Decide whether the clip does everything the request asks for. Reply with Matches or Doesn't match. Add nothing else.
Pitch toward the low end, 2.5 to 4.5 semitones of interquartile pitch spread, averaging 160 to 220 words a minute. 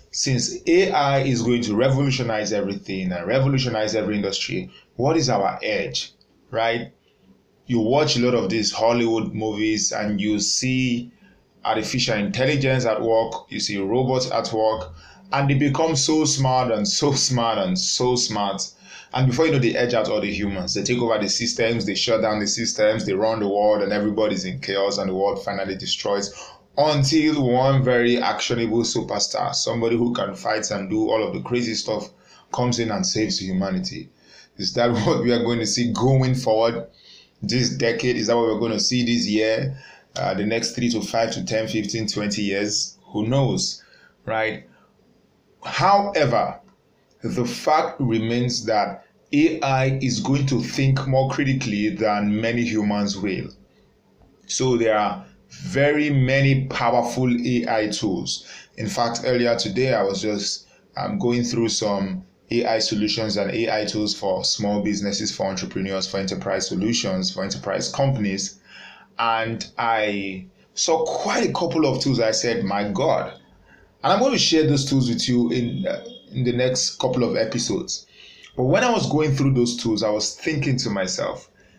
Matches